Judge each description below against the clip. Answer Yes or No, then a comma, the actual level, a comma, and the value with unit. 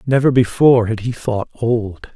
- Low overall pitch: Yes, low, 120 Hz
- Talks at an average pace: Yes, average, 165 wpm